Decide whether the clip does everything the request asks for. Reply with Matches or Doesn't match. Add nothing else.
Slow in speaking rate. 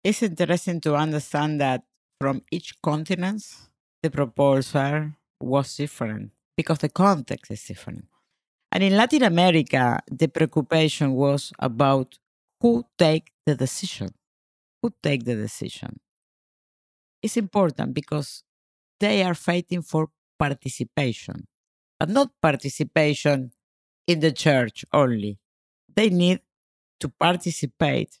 Matches